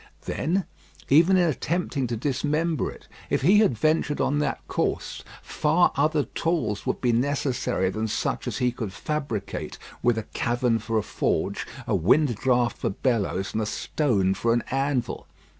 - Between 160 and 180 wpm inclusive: Yes, average, 165 wpm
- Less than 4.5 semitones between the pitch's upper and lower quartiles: No, average, 5.0 semitones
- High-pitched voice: No, low, 130 Hz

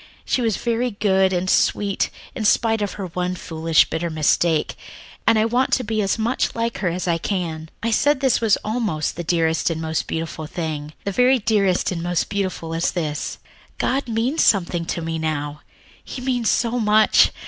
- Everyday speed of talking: Yes, average, 190 wpm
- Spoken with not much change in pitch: No, wide, 5.6 semitones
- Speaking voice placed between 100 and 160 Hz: No, high, 190 Hz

